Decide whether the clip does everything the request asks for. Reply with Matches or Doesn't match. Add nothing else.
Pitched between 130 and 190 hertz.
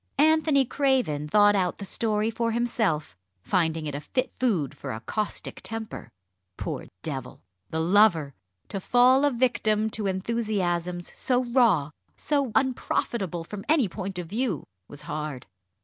Doesn't match